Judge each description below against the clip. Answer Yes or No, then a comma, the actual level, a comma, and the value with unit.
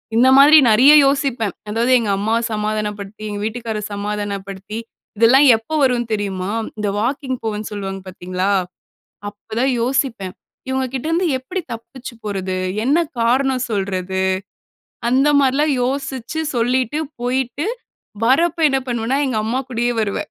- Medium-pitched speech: No, high, 235 Hz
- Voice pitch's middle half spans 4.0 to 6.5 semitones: Yes, average, 4.3 semitones